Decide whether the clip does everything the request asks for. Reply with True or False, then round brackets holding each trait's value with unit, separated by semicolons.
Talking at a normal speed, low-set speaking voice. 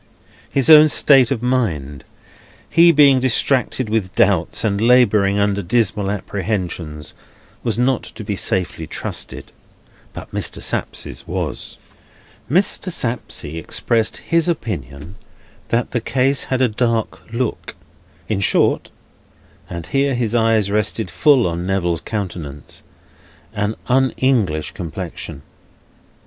False (120 wpm; 110 Hz)